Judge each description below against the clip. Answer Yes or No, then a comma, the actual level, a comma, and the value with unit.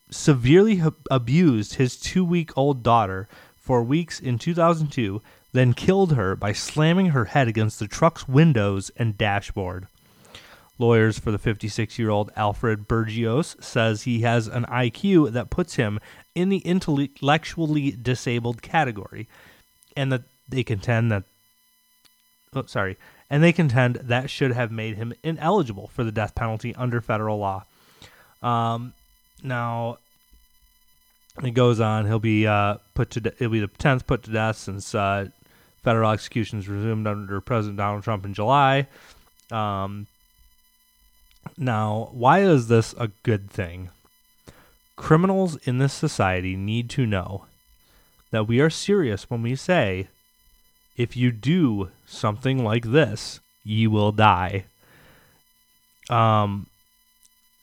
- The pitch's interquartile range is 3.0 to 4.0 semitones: No, average, 4.4 semitones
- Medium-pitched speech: No, low, 115 Hz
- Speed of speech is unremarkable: No, slow, 130 wpm